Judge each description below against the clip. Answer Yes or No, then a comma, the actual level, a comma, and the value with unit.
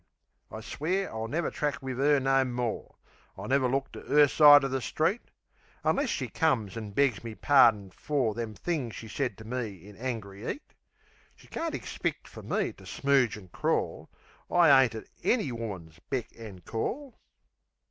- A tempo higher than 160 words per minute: Yes, average, 175 wpm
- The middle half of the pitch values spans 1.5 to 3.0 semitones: No, average, 4.6 semitones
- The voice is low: Yes, low, 125 Hz